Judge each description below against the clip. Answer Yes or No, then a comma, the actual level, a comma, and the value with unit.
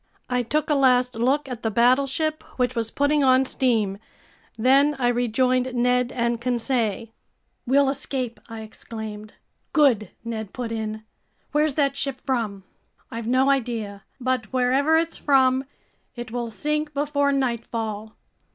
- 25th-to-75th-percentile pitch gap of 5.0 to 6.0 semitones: No, average, 3.2 semitones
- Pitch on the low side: No, very high, 250 Hz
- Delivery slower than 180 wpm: Yes, average, 140 wpm